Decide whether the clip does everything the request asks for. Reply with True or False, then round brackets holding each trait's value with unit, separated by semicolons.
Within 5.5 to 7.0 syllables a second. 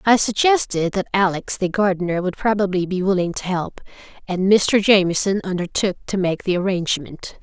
False (5.3 syllables/s)